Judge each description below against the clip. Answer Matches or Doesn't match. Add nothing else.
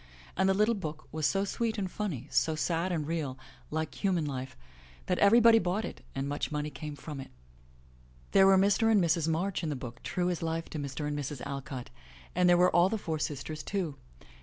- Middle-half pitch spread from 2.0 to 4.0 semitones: Doesn't match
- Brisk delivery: Matches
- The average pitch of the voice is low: Doesn't match